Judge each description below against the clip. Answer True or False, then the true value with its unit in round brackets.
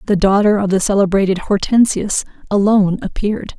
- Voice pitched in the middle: False (200 Hz)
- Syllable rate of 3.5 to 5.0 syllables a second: False (5.8 syllables/s)